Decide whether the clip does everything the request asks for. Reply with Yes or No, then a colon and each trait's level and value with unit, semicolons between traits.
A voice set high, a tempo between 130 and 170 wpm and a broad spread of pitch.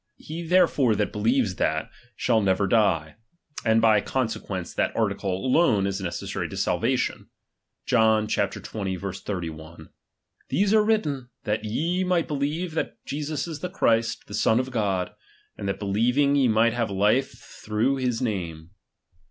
No: low, 110 Hz; average, 155 wpm; wide, 6.0 semitones